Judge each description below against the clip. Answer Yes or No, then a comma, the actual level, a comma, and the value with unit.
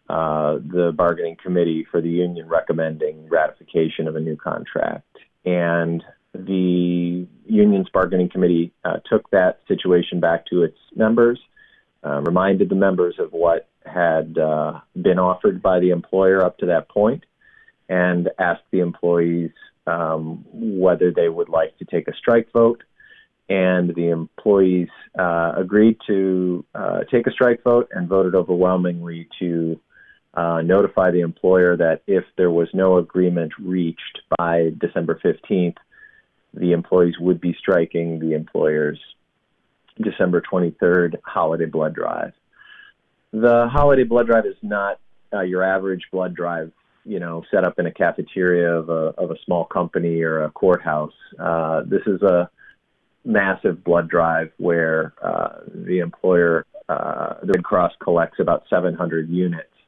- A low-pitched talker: Yes, very low, 90 Hz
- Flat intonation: Yes, narrow, 2.2 semitones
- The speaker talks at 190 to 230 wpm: No, average, 145 wpm